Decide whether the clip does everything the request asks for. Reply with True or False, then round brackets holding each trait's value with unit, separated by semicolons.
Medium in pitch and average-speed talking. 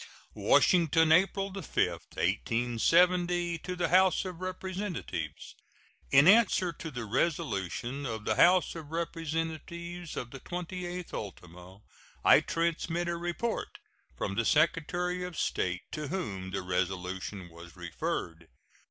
False (165 Hz; 120 wpm)